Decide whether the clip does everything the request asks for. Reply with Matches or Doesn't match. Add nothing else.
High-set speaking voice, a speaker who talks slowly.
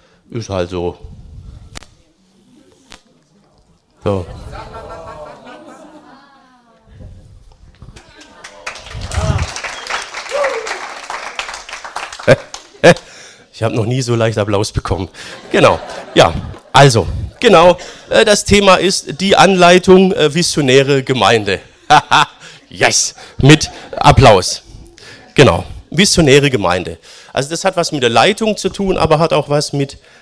Doesn't match